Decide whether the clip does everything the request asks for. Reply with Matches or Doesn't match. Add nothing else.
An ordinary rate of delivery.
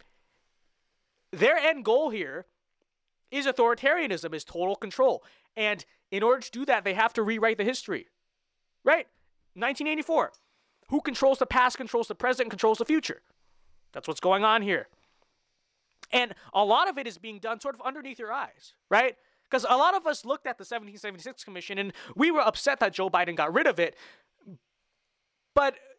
Matches